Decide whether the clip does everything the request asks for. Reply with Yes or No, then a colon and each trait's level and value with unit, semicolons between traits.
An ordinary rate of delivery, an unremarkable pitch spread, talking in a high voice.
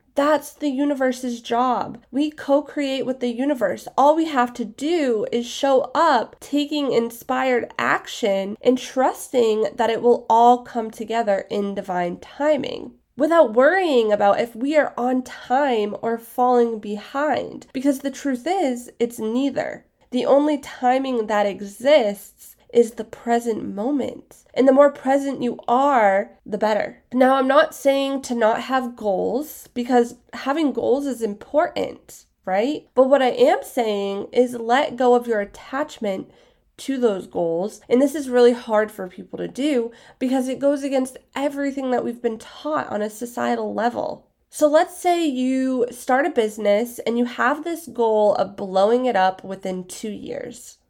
Yes: average, 160 wpm; average, 3.7 semitones; very high, 250 Hz